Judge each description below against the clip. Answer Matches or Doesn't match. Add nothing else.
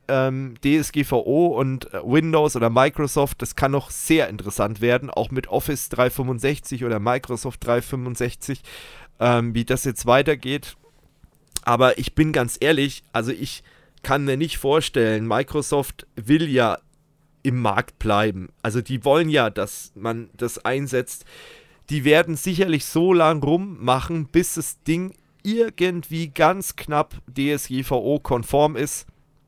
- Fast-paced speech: Doesn't match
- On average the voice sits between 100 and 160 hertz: Matches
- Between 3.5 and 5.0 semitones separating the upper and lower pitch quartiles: Matches